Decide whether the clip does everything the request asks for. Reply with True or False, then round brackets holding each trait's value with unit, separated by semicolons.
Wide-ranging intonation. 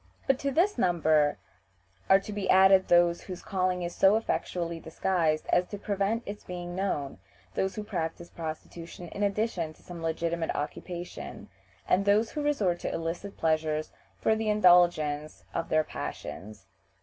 False (3.5 semitones)